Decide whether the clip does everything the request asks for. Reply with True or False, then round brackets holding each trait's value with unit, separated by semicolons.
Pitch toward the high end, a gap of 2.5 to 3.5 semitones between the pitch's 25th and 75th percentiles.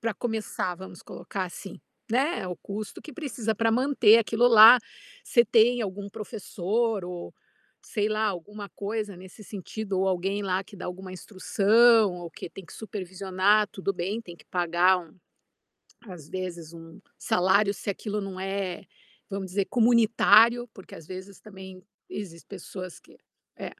True (200 Hz; 3.0 semitones)